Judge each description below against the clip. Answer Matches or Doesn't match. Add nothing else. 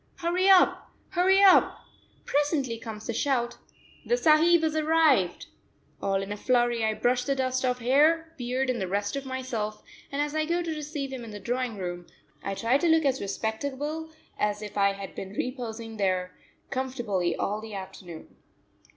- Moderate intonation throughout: Doesn't match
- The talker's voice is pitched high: Matches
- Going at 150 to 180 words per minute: Matches